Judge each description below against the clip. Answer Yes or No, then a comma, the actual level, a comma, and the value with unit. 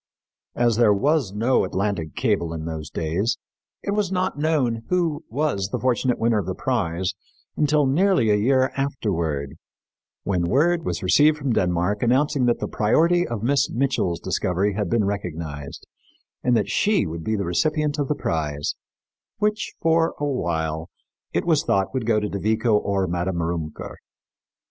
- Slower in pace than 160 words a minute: No, average, 165 wpm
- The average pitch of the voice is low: Yes, low, 110 Hz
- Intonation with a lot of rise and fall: Yes, wide, 8.4 semitones